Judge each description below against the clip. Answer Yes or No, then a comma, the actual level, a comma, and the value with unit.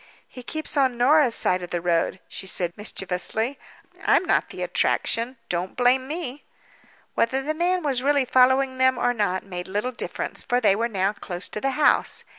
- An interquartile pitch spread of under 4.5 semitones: No, wide, 5.6 semitones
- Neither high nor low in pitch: No, high, 245 Hz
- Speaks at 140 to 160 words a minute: No, average, 180 wpm